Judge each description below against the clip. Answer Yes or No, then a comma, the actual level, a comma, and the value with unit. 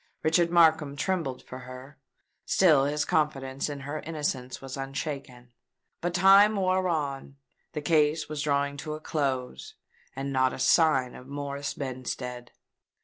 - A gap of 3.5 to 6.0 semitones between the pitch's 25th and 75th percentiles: No, average, 2.9 semitones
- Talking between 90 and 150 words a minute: Yes, average, 140 wpm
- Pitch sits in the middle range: Yes, medium, 145 Hz